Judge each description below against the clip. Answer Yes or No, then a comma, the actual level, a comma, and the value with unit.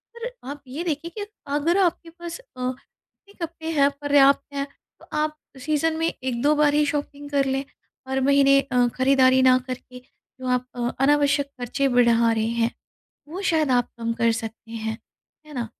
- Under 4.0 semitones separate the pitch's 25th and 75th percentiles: Yes, average, 3.3 semitones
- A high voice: Yes, very high, 275 Hz